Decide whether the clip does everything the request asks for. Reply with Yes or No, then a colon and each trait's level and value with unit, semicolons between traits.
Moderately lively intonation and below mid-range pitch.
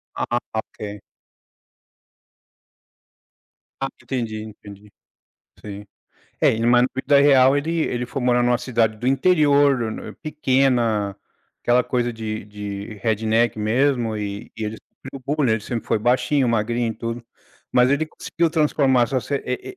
Yes: average, 3.6 semitones; low, 120 Hz